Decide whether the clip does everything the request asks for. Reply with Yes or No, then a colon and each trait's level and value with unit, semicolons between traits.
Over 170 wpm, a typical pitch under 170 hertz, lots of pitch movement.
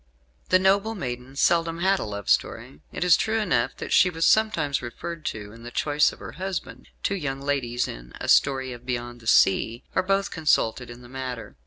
Yes: fast, 205 wpm; low, 135 Hz; wide, 6.9 semitones